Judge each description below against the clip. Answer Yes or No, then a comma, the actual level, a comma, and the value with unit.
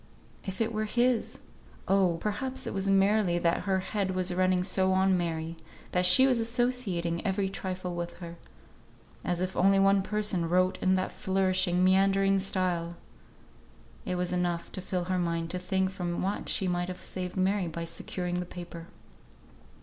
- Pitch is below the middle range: No, medium, 185 Hz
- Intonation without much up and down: Yes, narrow, 1.7 semitones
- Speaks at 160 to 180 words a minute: Yes, average, 170 wpm